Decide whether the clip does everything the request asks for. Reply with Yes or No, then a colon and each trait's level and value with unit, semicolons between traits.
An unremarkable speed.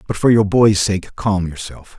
No: fast, 210 wpm